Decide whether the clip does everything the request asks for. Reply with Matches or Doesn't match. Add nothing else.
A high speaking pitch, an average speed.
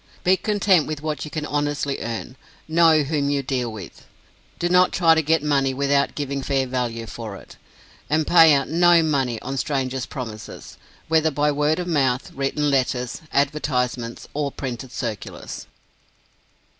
Doesn't match